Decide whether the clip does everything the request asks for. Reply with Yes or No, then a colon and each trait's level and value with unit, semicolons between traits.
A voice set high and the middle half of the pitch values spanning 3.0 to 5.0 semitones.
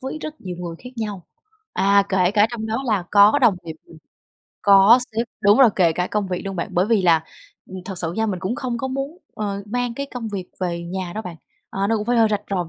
Yes: high, 205 Hz; average, 4.0 semitones